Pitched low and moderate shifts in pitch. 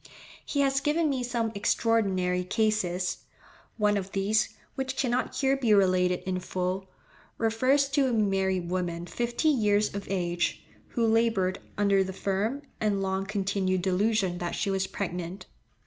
No: high, 200 Hz; average, 3.6 semitones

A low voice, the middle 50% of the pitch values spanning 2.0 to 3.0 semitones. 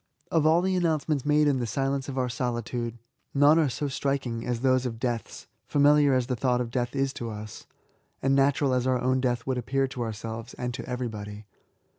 Yes: low, 130 Hz; narrow, 2.6 semitones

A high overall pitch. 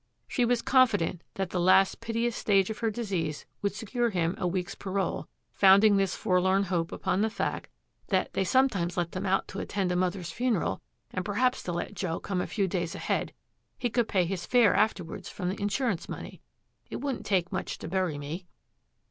Yes: high, 195 Hz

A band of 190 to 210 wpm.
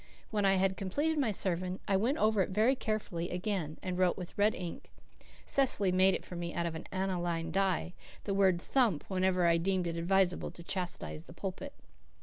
Yes: average, 195 wpm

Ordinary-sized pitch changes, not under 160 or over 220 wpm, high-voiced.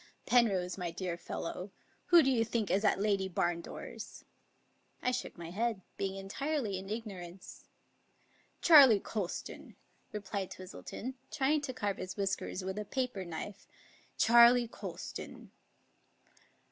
No: average, 4.1 semitones; slow, 135 wpm; high, 205 Hz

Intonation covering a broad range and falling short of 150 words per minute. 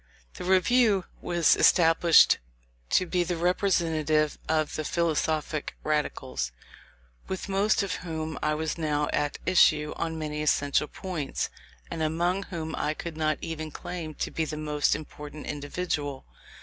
No: narrow, 2.5 semitones; average, 140 wpm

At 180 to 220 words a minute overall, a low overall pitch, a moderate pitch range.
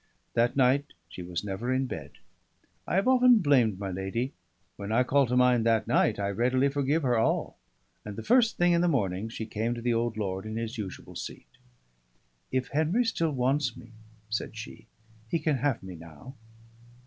Yes: average, 190 wpm; low, 120 Hz; average, 4.8 semitones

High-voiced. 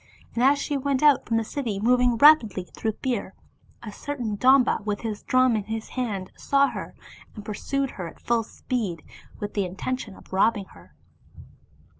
Yes: high, 230 Hz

